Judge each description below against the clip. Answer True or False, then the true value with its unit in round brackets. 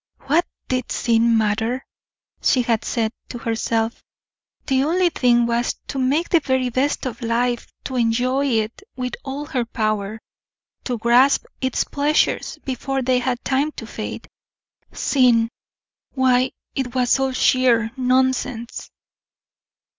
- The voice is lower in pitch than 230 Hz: False (250 Hz)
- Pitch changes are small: True (2.3 semitones)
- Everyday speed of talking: False (130 wpm)